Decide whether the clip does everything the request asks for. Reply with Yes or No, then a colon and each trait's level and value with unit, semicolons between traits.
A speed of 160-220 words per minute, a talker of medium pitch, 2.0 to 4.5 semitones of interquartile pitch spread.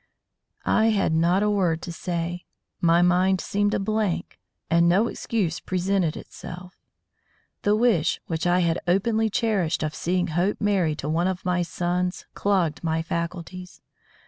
No: average, 150 wpm; medium, 180 Hz; average, 2.8 semitones